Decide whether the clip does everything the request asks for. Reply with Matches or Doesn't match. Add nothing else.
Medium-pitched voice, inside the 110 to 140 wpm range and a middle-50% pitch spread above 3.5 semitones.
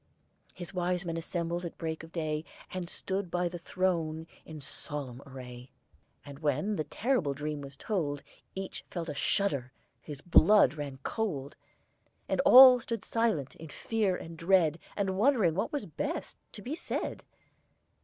Doesn't match